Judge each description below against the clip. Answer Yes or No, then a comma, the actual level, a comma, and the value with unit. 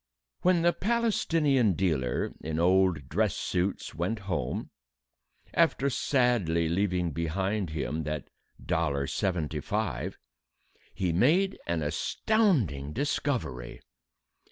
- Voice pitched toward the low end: Yes, very low, 90 Hz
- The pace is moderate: No, slow, 100 wpm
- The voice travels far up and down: Yes, wide, 8.7 semitones